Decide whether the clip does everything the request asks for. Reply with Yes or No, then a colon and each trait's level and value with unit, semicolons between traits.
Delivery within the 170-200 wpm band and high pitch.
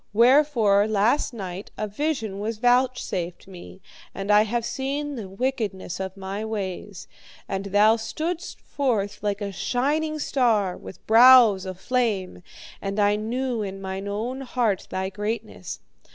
No: average, 140 wpm; high, 215 Hz